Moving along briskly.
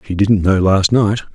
Yes: fast, 225 wpm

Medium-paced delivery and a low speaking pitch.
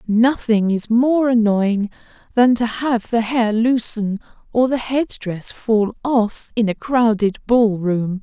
No: average, 155 wpm; high, 225 Hz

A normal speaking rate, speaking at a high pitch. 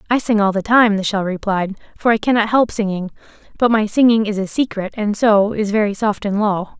No: fast, 230 wpm; high, 210 Hz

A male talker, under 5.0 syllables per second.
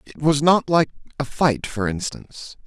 Yes: male; 4.6 syllables/s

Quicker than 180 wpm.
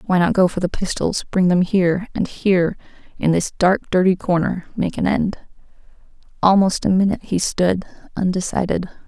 No: average, 165 wpm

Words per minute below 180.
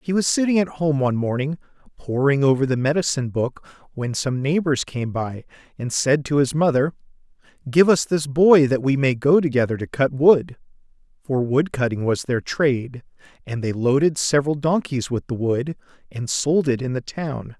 No: average, 185 wpm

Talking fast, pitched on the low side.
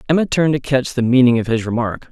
Yes: fast, 255 wpm; low, 130 Hz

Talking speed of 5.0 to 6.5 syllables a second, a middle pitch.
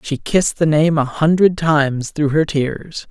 No: 4.3 syllables/s; medium, 155 Hz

